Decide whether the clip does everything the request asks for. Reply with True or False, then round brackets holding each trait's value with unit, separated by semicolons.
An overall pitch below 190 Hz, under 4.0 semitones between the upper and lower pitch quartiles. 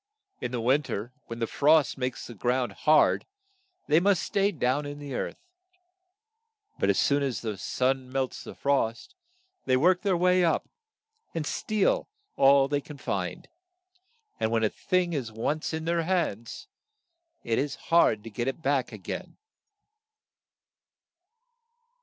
False (140 Hz; 5.0 semitones)